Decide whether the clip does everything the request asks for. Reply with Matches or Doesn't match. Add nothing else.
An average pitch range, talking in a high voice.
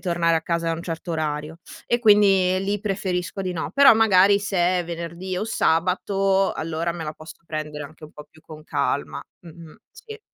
Doesn't match